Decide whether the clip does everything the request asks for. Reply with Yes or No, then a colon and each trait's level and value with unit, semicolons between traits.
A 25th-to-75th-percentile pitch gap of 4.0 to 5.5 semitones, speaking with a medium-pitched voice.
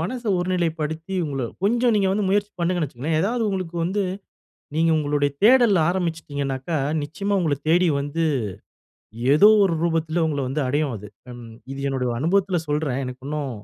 Yes: average, 4.7 semitones; medium, 165 Hz